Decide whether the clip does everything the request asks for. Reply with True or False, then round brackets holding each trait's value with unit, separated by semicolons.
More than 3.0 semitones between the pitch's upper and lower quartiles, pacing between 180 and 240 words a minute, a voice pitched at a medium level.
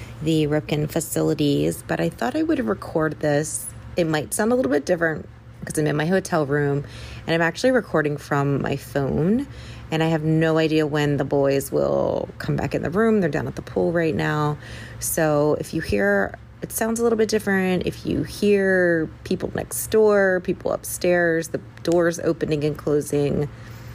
True (3.6 semitones; 185 wpm; 155 Hz)